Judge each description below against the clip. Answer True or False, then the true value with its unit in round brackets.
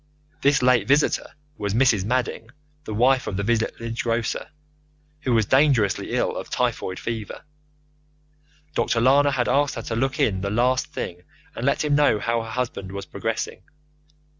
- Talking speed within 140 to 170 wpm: True (165 wpm)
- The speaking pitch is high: False (115 Hz)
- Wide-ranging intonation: False (3.5 semitones)